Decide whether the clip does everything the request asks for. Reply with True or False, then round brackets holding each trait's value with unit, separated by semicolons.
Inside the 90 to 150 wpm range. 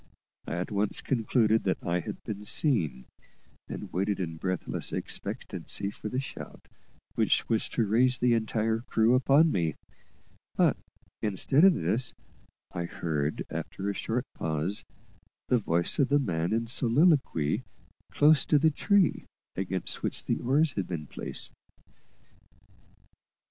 True (140 wpm)